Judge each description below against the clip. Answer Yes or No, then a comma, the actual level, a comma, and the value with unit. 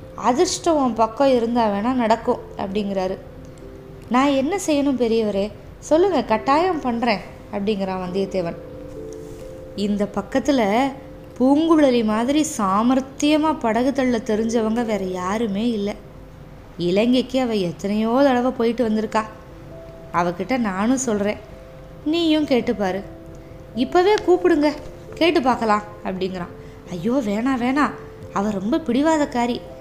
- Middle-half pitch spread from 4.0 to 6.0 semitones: Yes, average, 5.1 semitones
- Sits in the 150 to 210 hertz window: No, high, 235 Hz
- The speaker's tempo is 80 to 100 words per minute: Yes, average, 95 wpm